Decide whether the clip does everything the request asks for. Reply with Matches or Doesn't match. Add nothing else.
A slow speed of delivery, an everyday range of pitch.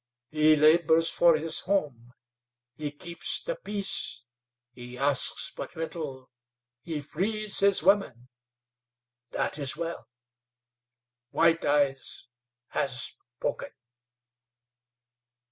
Matches